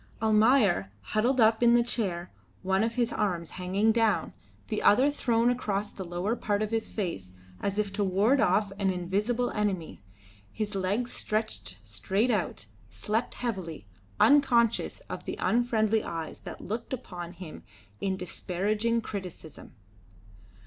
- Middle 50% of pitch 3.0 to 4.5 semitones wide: Yes, average, 3.8 semitones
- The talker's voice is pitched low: No, high, 210 Hz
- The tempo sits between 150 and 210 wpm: No, average, 140 wpm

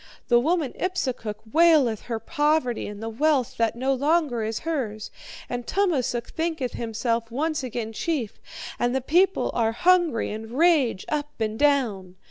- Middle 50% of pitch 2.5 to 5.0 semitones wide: No, wide, 5.5 semitones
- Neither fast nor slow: Yes, average, 150 wpm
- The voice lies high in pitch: Yes, very high, 250 Hz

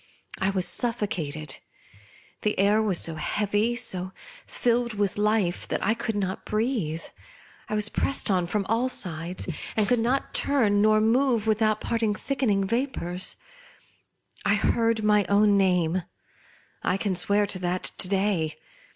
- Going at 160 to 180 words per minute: No, average, 150 wpm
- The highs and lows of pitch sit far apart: No, average, 3.2 semitones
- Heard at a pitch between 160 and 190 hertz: No, high, 205 Hz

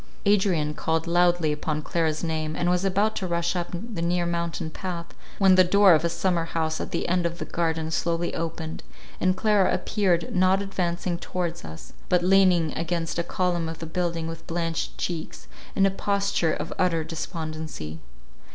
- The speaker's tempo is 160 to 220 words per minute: Yes, average, 180 wpm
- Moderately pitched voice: Yes, medium, 170 Hz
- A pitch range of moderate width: No, narrow, 2.2 semitones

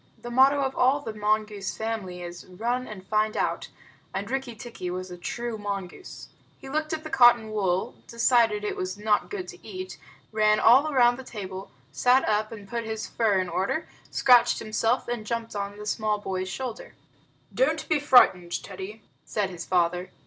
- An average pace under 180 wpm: No, average, 185 wpm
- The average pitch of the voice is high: Yes, high, 215 Hz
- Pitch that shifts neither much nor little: Yes, average, 3.9 semitones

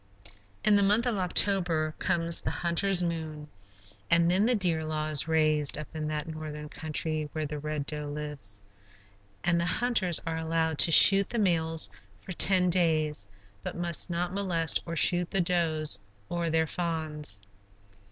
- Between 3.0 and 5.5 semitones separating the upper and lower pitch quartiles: No, narrow, 2.5 semitones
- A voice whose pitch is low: No, medium, 165 Hz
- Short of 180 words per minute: Yes, average, 160 wpm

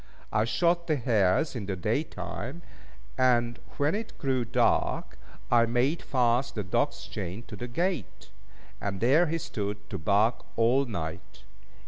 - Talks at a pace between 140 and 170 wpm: Yes, average, 150 wpm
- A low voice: Yes, low, 120 Hz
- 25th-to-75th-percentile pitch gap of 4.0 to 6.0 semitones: Yes, average, 5.1 semitones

